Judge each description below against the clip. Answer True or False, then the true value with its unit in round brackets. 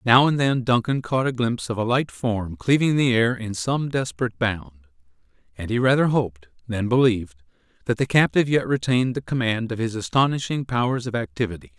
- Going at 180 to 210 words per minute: True (190 wpm)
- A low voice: True (120 Hz)